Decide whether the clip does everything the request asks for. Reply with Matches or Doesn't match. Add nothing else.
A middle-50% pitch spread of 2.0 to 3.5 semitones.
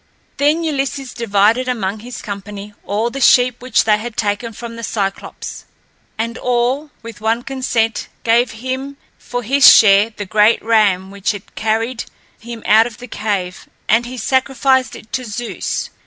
Matches